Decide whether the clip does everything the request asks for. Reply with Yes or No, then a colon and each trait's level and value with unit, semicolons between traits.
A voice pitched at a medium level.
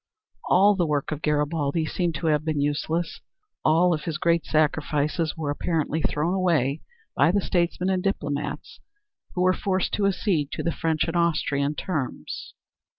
Yes: medium, 160 Hz